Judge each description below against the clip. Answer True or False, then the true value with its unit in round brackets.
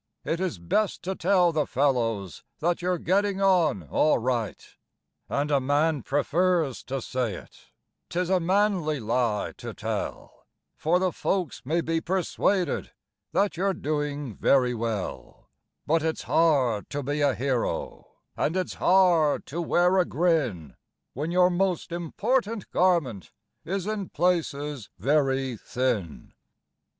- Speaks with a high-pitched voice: False (155 Hz)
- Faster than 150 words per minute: False (135 wpm)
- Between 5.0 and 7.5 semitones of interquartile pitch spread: True (5.6 semitones)